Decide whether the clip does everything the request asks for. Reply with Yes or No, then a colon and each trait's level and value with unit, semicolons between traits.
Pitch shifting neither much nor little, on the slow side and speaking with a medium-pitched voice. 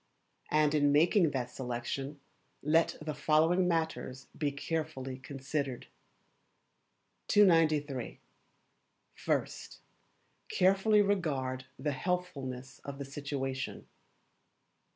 Yes: average, 3.4 semitones; slow, 85 wpm; medium, 145 Hz